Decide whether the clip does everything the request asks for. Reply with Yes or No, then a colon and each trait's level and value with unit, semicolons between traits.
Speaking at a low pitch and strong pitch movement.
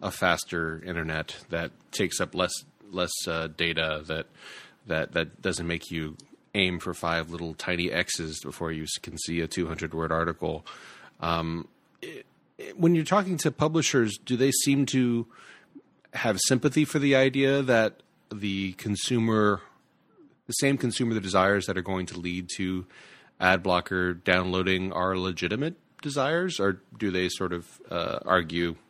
Yes: very low, 95 Hz; wide, 6.2 semitones